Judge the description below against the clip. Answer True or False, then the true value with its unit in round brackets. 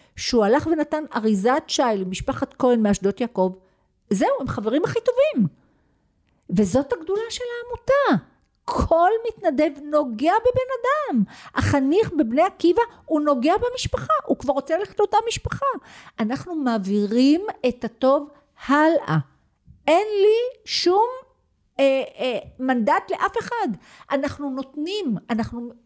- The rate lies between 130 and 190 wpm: False (120 wpm)